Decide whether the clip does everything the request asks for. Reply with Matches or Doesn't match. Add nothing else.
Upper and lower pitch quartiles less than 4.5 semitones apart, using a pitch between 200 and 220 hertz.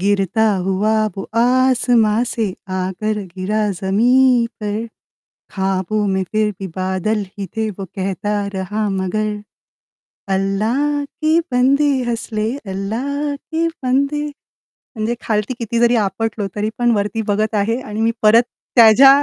Matches